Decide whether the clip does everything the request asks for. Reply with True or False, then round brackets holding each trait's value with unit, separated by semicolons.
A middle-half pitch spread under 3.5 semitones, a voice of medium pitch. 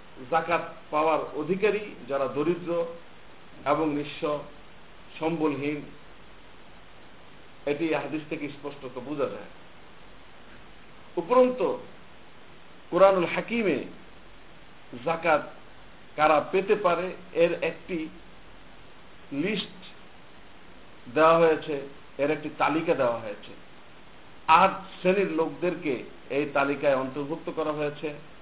True (2.7 semitones; 155 Hz)